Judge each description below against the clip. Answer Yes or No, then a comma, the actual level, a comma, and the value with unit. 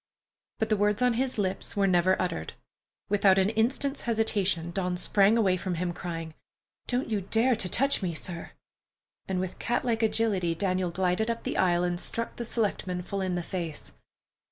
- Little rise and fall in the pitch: No, average, 3.8 semitones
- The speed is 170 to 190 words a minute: Yes, average, 180 wpm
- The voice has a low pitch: No, high, 190 Hz